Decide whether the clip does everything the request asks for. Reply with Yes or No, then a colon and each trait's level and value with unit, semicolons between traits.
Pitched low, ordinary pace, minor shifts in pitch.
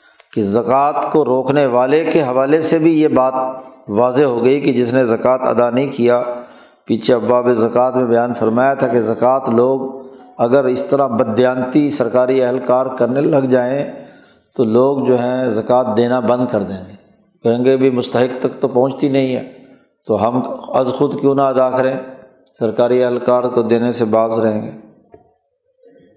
Yes: low, 125 Hz; average, 170 wpm; narrow, 1.6 semitones